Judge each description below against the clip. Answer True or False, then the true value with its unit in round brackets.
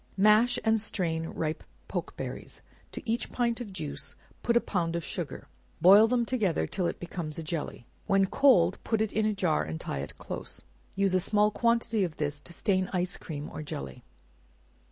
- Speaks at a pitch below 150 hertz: False (190 Hz)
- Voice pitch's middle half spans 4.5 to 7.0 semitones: True (5.2 semitones)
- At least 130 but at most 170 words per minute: False (185 wpm)